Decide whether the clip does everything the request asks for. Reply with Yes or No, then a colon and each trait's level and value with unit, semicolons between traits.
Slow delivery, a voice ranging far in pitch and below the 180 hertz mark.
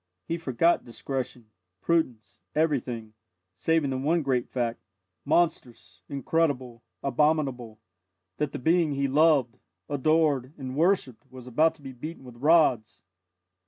No: slow, 125 wpm; average, 4.4 semitones; low, 135 Hz